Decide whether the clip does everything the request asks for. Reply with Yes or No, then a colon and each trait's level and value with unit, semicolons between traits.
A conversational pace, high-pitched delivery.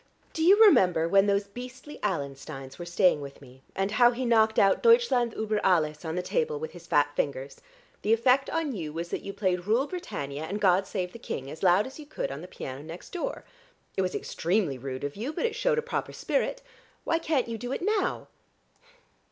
No: fast, 215 wpm; high, 205 Hz